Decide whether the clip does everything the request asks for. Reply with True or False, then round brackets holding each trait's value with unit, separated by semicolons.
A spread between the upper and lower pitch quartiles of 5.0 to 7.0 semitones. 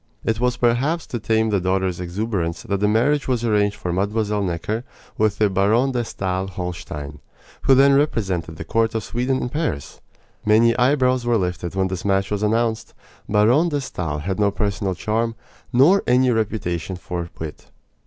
False (4.3 semitones)